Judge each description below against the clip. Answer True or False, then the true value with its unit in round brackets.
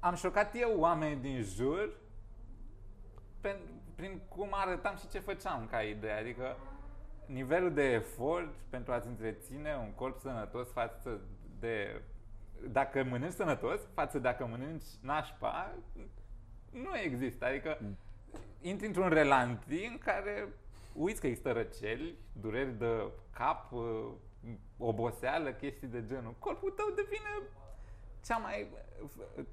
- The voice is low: True (125 Hz)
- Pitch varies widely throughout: True (6.1 semitones)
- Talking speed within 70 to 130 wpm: True (120 wpm)